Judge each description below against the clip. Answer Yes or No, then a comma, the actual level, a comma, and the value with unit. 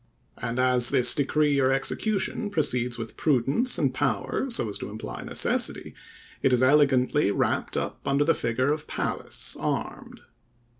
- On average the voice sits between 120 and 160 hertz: Yes, low, 135 Hz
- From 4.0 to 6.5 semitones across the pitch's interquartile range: No, average, 3.3 semitones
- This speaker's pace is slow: No, average, 150 wpm